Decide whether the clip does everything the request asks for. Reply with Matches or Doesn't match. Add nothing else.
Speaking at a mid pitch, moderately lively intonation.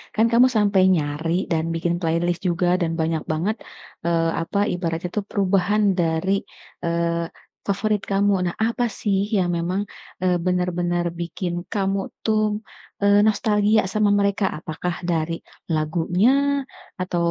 Matches